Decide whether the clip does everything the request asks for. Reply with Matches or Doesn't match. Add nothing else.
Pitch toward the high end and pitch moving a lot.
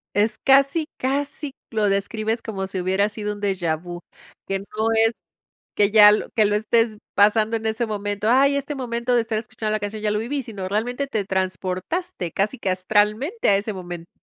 Doesn't match